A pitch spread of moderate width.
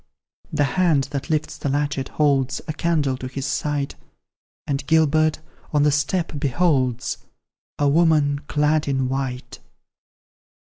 No: narrow, 2.3 semitones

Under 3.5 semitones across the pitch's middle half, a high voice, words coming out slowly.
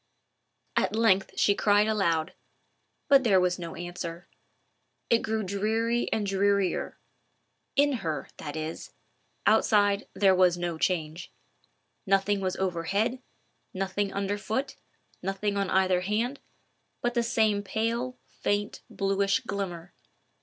Yes: average, 3.1 semitones; high, 200 Hz; slow, 120 wpm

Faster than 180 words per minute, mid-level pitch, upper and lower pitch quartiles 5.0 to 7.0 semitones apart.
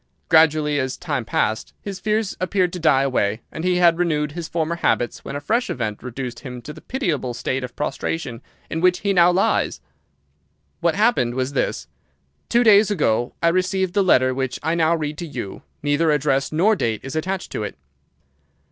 Yes: average, 190 wpm; medium, 155 Hz; wide, 5.6 semitones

